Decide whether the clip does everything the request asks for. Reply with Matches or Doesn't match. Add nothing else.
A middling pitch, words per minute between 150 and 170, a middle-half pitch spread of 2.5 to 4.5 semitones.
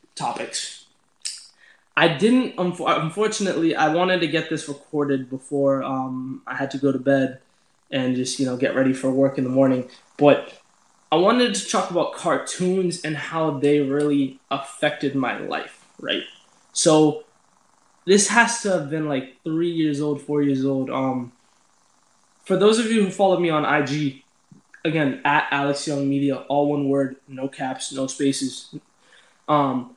Matches